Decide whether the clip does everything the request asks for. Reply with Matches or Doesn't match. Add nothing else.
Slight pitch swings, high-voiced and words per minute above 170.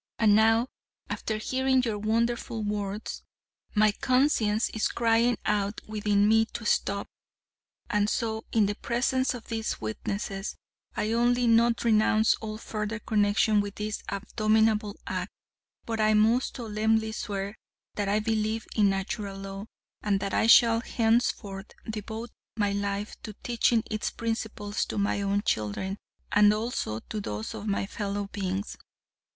Doesn't match